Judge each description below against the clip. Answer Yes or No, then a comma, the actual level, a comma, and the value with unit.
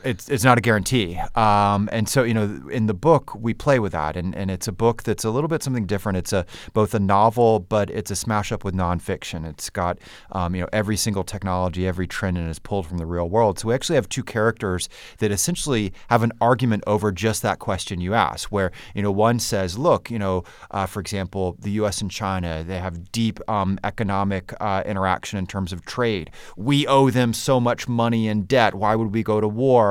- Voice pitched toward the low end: Yes, low, 105 Hz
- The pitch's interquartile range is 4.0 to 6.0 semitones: No, average, 3.3 semitones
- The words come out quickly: Yes, fast, 230 wpm